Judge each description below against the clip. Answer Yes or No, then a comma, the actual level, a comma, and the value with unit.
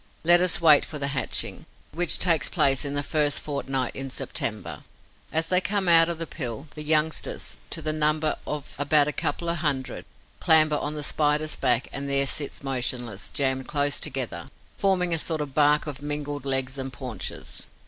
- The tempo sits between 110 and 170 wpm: No, average, 185 wpm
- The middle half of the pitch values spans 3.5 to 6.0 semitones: No, narrow, 2.6 semitones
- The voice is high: No, medium, 145 Hz